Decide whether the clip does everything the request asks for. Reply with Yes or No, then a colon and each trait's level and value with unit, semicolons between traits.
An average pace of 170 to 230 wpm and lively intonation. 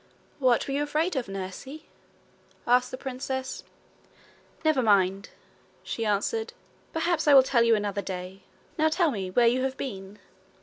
No: average, 150 wpm; wide, 6.2 semitones